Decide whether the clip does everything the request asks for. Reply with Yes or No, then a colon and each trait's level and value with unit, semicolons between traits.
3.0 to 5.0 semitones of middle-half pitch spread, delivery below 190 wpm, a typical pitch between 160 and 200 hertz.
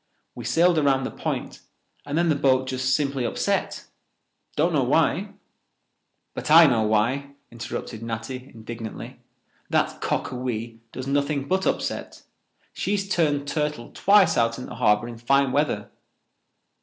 No: average, 4.0 semitones; average, 140 wpm; low, 130 Hz